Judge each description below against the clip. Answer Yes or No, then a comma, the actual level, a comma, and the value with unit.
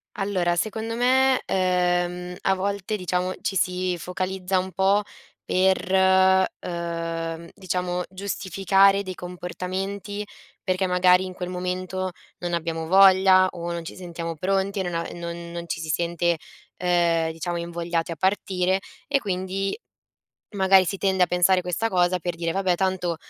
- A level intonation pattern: Yes, narrow, 1.8 semitones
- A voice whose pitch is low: No, medium, 185 Hz